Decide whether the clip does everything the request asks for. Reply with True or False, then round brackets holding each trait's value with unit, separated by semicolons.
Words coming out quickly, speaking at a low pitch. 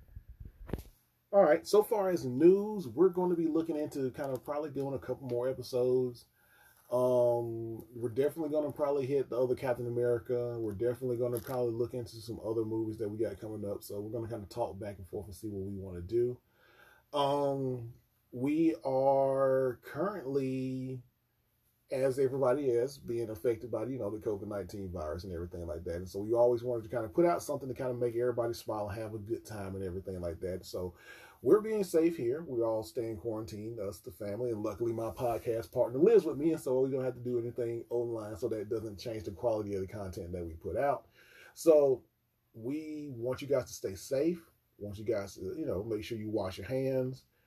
True (220 wpm; 120 Hz)